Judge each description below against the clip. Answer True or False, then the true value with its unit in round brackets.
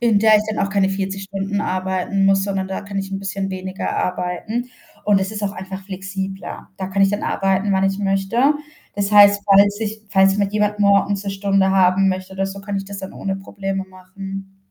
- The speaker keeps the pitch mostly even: True (0.9 semitones)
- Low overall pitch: False (195 Hz)